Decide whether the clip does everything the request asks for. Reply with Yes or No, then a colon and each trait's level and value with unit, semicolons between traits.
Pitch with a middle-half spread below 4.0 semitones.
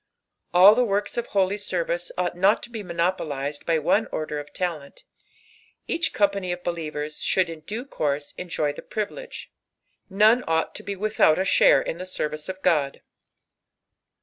No: average, 4.5 semitones